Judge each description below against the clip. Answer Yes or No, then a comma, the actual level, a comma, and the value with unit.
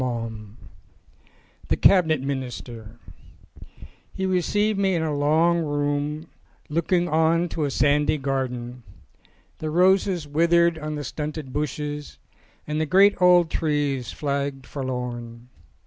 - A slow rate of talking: Yes, slow, 120 wpm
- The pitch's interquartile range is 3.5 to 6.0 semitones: Yes, average, 3.9 semitones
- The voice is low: No, medium, 150 Hz